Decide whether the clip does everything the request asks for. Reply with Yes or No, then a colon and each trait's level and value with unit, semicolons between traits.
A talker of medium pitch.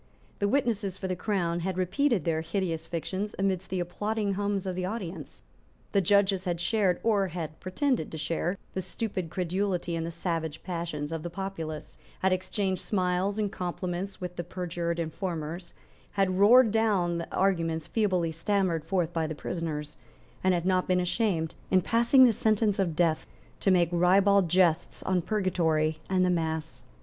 Yes: medium, 180 Hz